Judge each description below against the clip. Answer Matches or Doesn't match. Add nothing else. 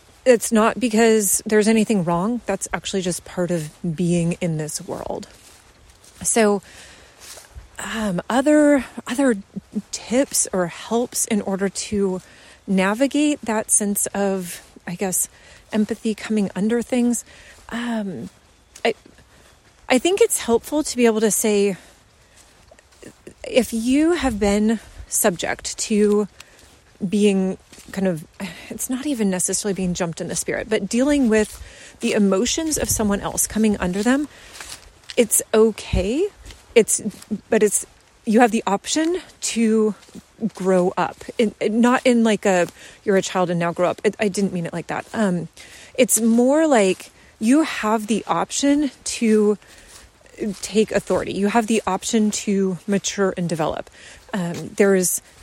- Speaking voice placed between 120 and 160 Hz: Doesn't match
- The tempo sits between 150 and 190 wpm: Doesn't match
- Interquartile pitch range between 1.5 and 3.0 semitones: Doesn't match